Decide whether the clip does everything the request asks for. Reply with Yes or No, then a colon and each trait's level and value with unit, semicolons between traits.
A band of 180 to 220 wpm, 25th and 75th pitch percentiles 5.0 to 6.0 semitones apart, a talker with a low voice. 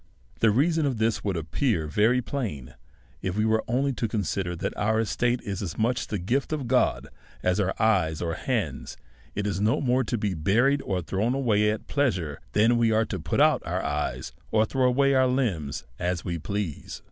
Yes: fast, 205 wpm; wide, 5.4 semitones; low, 110 Hz